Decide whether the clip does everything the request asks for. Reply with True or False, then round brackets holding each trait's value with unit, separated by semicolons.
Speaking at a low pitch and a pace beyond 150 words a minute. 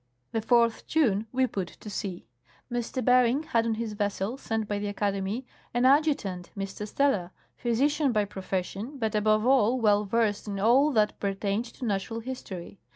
False (220 Hz; 165 wpm)